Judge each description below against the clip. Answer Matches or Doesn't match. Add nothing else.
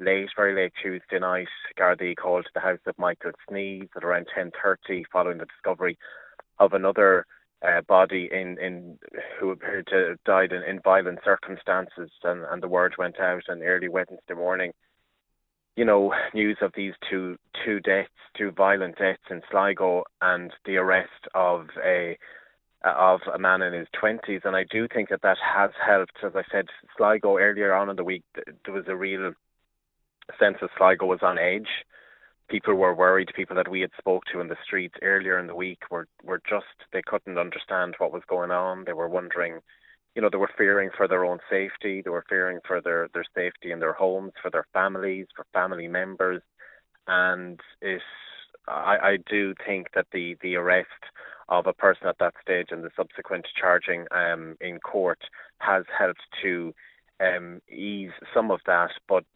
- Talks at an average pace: Matches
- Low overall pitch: Matches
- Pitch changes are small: Matches